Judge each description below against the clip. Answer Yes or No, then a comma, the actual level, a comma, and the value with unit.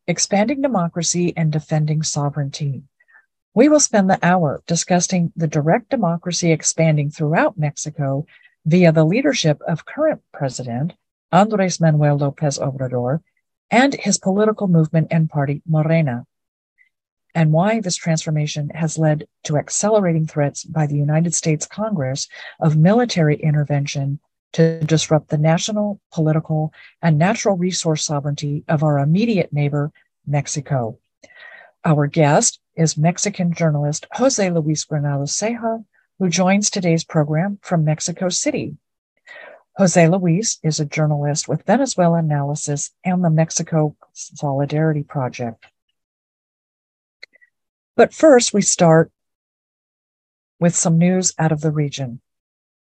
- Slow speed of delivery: Yes, slow, 120 wpm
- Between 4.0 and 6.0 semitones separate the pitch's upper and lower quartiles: No, average, 3.4 semitones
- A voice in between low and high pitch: Yes, medium, 160 Hz